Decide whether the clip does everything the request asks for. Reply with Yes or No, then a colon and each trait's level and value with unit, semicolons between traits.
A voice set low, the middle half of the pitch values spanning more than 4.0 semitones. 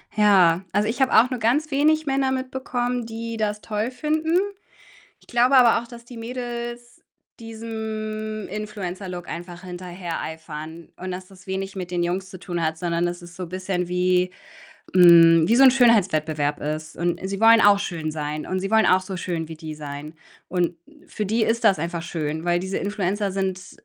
No: high, 190 Hz; average, 4.7 semitones